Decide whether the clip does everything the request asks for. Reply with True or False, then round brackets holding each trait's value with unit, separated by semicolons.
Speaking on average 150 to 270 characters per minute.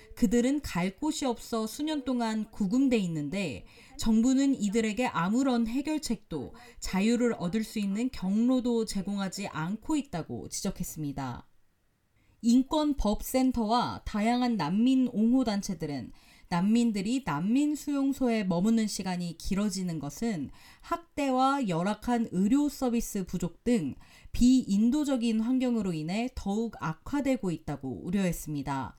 False (285 characters per minute)